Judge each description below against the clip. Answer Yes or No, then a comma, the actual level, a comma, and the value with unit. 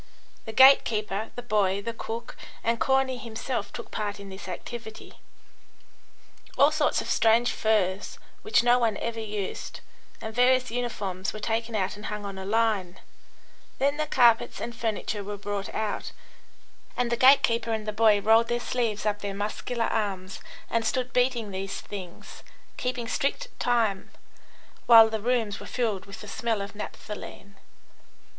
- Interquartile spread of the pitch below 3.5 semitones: Yes, average, 2.8 semitones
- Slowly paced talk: No, average, 160 wpm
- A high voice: Yes, high, 225 Hz